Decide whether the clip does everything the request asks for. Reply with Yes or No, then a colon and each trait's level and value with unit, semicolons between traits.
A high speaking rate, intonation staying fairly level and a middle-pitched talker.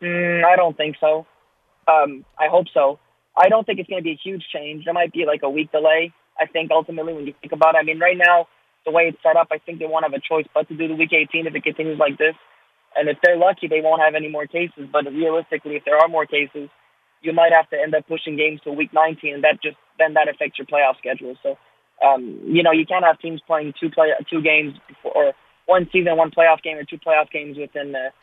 Yes: fast, 265 wpm; narrow, 1.7 semitones; medium, 160 Hz